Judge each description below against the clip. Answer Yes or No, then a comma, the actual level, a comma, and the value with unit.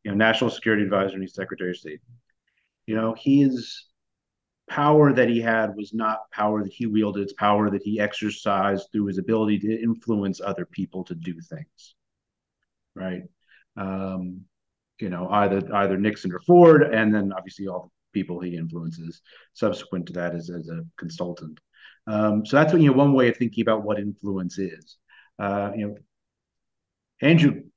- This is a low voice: Yes, low, 105 Hz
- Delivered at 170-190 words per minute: Yes, average, 175 wpm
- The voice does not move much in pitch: No, average, 3.0 semitones